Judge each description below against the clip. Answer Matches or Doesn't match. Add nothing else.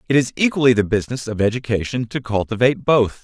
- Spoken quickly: Doesn't match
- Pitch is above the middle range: Doesn't match